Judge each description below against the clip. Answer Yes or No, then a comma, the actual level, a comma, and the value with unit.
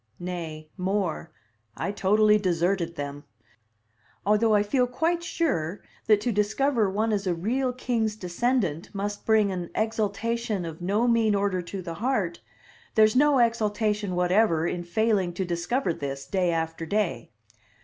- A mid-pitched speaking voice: No, high, 205 Hz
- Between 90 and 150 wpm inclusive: Yes, average, 145 wpm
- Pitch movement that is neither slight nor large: Yes, average, 4.2 semitones